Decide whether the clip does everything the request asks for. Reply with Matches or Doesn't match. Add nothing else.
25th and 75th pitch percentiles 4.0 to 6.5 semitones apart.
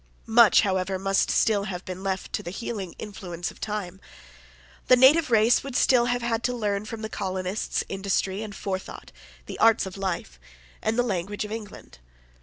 Doesn't match